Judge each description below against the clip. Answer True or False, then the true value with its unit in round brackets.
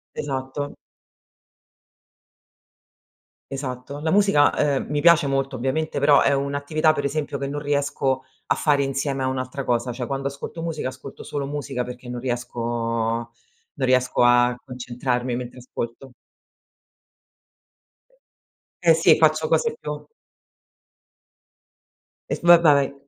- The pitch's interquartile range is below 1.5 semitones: False (2.5 semitones)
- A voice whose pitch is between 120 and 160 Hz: True (140 Hz)